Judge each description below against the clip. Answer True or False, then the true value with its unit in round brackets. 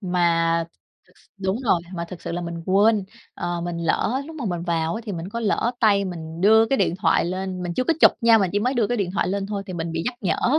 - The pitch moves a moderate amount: True (4.3 semitones)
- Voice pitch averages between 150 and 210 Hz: True (190 Hz)